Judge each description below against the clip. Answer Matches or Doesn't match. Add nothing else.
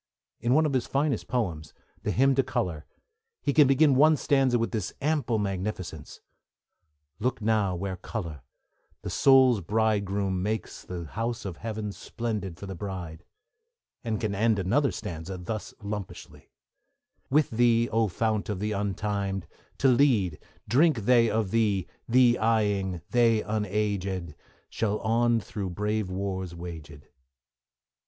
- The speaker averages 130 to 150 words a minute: Matches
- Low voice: Matches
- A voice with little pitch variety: Doesn't match